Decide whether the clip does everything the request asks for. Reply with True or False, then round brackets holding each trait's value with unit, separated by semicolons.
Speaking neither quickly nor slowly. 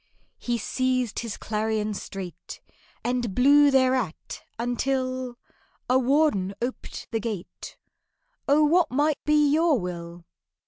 False (110 wpm)